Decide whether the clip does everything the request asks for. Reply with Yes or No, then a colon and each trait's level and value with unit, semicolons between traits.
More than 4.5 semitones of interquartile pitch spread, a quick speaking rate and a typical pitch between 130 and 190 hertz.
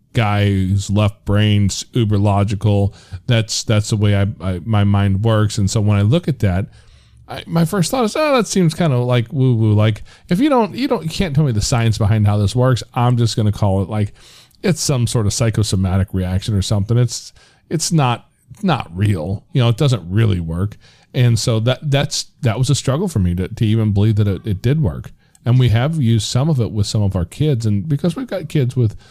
No: average, 5.2 semitones; fast, 235 wpm; low, 115 Hz